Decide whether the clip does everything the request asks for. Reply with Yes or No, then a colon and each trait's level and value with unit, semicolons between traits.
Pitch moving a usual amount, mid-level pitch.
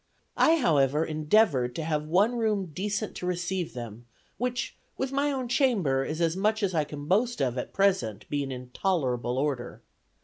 No: wide, 7.6 semitones; medium, 165 Hz